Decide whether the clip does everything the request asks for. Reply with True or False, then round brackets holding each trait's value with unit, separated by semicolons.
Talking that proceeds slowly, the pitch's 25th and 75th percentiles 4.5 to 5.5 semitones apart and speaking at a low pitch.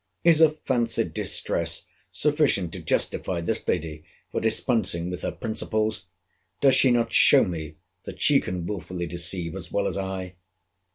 False (155 wpm; 5.2 semitones; 95 Hz)